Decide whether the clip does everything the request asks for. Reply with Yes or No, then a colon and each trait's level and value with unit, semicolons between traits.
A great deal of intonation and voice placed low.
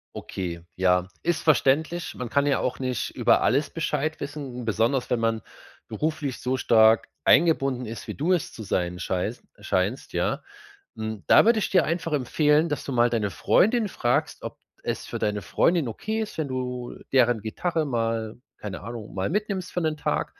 Yes: wide, 5.9 semitones; low, 130 Hz